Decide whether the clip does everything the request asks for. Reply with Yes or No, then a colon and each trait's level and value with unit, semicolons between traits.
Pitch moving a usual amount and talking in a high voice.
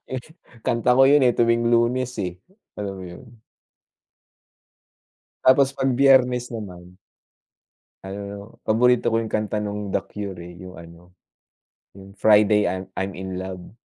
No: average, 4.6 semitones; low, 105 Hz